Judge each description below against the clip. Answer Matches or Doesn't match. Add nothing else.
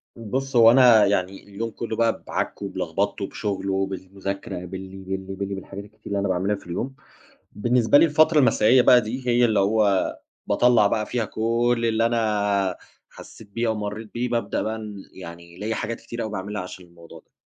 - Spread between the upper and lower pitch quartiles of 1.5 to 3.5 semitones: Matches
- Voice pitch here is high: Doesn't match